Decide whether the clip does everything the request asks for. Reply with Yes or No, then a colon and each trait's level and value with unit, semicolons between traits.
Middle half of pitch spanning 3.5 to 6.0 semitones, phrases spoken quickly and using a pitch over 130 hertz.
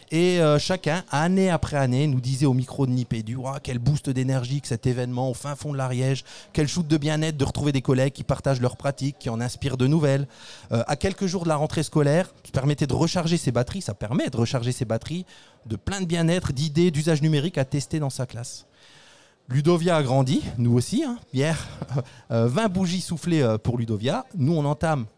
No: average, 3.9 semitones; average, 210 wpm; medium, 140 Hz